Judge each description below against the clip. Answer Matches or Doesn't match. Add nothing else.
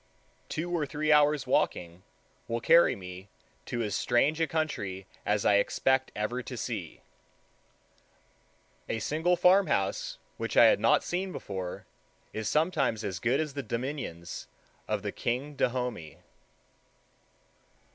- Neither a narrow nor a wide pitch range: Doesn't match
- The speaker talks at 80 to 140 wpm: Matches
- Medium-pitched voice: Doesn't match